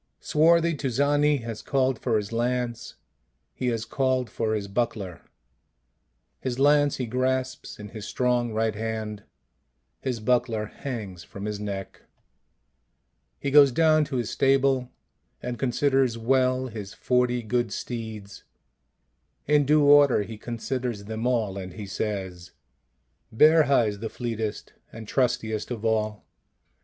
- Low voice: Yes, low, 120 Hz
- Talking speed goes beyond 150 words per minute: No, slow, 135 wpm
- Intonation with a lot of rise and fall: No, average, 3.4 semitones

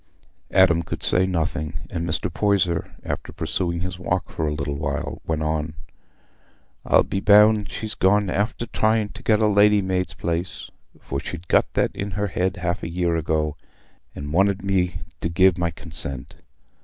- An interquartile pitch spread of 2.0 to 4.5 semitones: Yes, average, 3.3 semitones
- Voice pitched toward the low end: Yes, very low, 90 Hz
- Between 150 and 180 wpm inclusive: Yes, average, 170 wpm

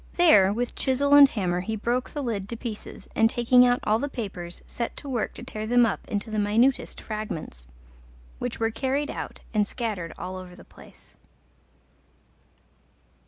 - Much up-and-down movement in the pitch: No, average, 3.5 semitones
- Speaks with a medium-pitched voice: No, high, 225 Hz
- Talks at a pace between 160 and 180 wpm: Yes, average, 170 wpm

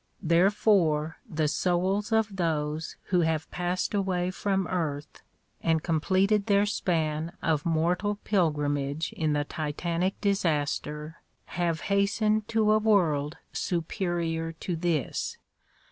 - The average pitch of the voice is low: No, medium, 170 Hz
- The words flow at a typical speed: No, slow, 125 wpm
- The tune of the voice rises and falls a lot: No, average, 3.9 semitones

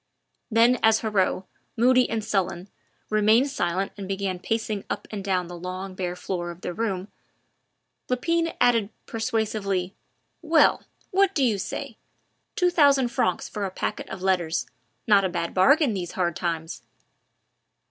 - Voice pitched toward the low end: No, high, 200 Hz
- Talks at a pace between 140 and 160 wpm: Yes, average, 145 wpm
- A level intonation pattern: No, average, 4.3 semitones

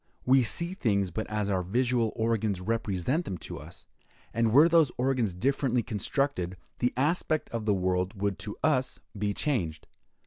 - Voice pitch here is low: Yes, low, 115 Hz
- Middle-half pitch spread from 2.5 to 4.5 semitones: No, average, 5.1 semitones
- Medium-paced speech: Yes, average, 165 wpm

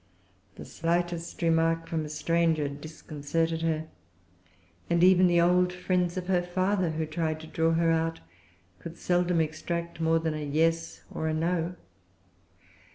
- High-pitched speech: No, medium, 165 Hz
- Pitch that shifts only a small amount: Yes, narrow, 1.6 semitones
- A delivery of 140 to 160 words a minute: Yes, average, 150 wpm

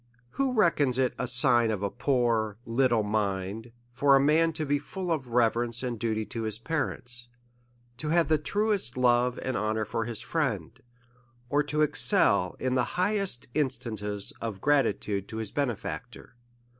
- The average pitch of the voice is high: No, low, 125 Hz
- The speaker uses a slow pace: No, average, 165 wpm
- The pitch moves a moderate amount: Yes, average, 4.8 semitones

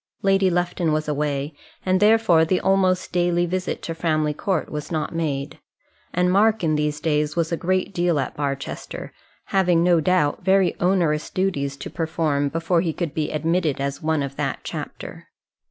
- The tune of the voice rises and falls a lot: No, average, 3.4 semitones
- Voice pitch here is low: No, medium, 165 Hz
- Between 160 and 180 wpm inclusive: Yes, average, 170 wpm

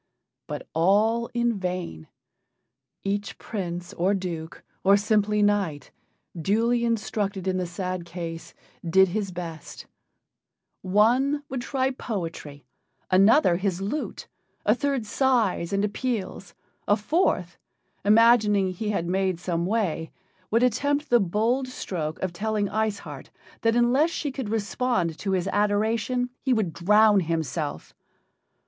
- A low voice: No, high, 205 Hz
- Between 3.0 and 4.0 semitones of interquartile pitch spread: No, average, 4.5 semitones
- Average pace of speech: No, slow, 130 wpm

